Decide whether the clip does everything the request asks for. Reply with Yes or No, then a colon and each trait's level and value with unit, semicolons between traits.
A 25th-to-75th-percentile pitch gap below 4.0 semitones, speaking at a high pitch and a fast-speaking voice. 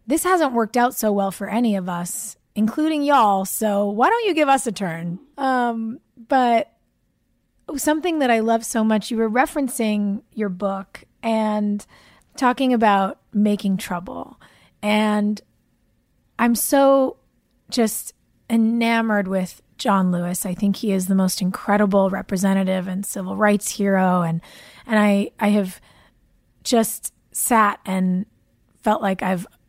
No: average, 3.4 semitones; high, 210 Hz; slow, 135 wpm